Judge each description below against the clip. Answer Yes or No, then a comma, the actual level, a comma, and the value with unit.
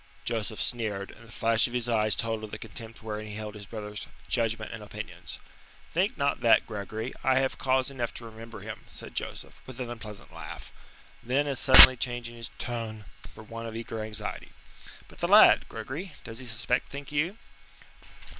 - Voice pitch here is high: No, low, 115 Hz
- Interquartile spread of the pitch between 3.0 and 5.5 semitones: No, narrow, 2.6 semitones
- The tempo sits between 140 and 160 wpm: No, average, 185 wpm